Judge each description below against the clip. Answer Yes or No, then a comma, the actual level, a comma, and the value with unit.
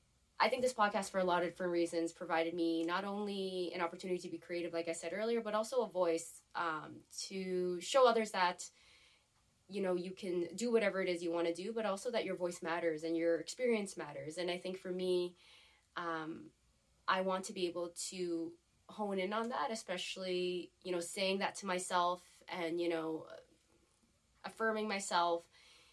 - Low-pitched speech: No, medium, 180 Hz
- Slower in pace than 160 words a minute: No, average, 190 wpm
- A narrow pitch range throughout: Yes, narrow, 2.3 semitones